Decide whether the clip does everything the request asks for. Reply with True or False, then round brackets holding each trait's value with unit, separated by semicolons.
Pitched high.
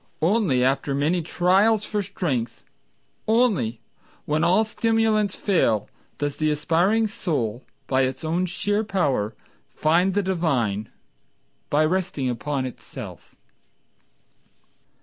False (165 Hz)